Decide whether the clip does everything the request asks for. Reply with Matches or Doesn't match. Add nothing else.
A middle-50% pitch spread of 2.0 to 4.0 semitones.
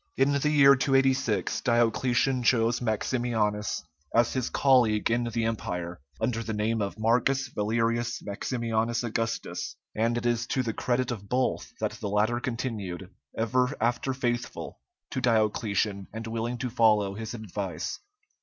Matches